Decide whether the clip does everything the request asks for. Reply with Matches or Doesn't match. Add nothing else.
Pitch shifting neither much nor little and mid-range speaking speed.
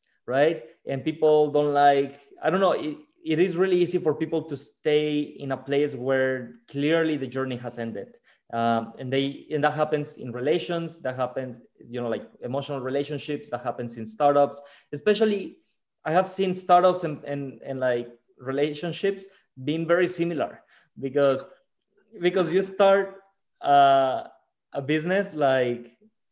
Matches